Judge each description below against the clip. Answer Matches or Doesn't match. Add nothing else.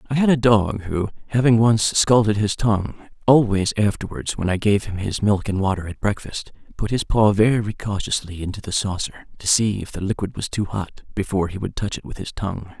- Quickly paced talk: Matches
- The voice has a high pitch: Doesn't match